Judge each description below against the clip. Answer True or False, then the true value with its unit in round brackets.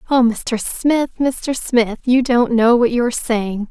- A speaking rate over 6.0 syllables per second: False (3.9 syllables/s)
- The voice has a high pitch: True (240 Hz)